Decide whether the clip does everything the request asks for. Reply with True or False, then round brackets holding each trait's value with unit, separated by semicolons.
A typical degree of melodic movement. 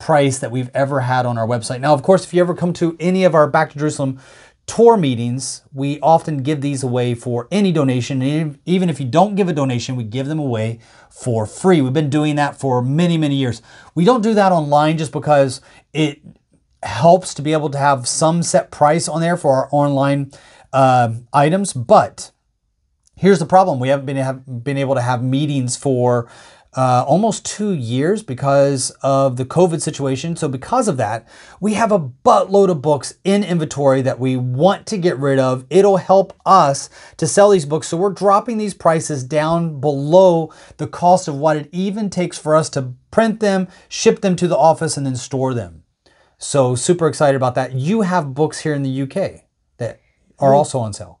True (4.9 semitones)